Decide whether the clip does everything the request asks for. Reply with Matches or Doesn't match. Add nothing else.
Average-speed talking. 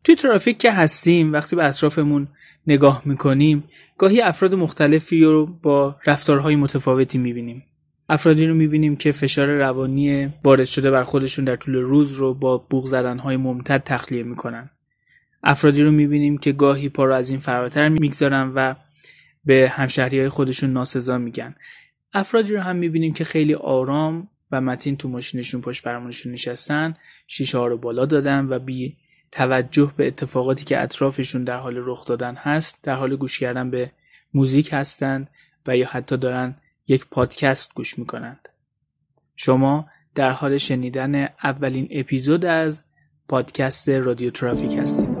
Matches